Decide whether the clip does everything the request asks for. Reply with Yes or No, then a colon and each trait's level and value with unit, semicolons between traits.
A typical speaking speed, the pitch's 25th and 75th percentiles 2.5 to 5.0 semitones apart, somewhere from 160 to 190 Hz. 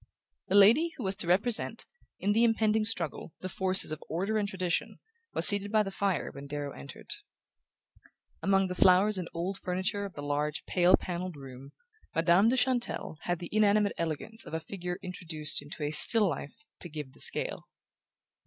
Yes: average, 180 wpm; average, 4.1 semitones; medium, 185 Hz